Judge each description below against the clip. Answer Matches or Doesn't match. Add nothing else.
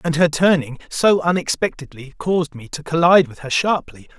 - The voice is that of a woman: Doesn't match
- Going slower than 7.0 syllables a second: Matches